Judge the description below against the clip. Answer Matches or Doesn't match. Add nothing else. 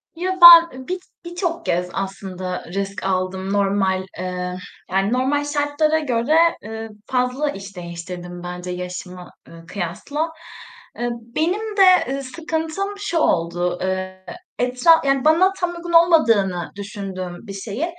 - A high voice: Matches